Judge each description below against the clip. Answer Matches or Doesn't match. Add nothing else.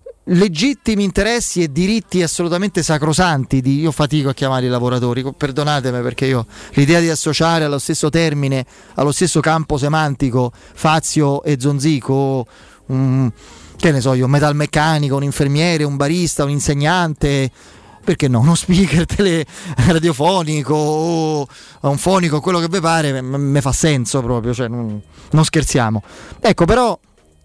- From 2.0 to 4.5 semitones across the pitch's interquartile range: Matches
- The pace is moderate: Matches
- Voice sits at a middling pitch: Matches